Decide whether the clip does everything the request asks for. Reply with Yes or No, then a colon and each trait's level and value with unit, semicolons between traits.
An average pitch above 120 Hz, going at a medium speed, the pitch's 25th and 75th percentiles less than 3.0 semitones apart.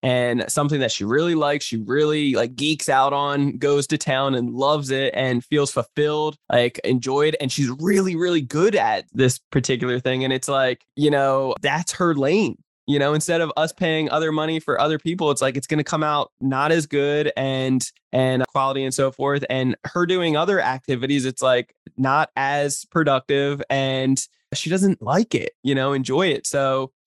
Yes: medium, 140 Hz; average, 195 wpm; narrow, 2.4 semitones